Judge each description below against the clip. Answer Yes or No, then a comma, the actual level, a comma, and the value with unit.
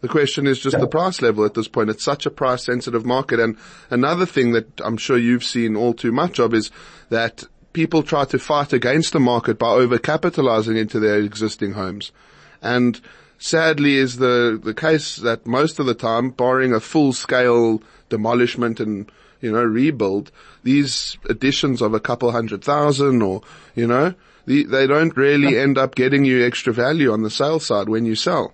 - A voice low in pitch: Yes, low, 125 Hz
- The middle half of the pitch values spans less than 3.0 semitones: No, average, 3.9 semitones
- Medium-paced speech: Yes, average, 190 wpm